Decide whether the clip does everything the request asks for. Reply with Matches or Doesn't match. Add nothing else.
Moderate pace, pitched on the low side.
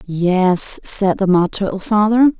Doesn't match